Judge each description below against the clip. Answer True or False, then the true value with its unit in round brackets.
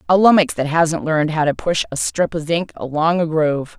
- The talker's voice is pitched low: False (160 Hz)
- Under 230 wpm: False (240 wpm)